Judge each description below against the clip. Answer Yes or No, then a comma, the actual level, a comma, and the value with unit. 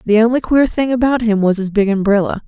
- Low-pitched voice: No, high, 220 Hz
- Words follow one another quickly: Yes, fast, 245 wpm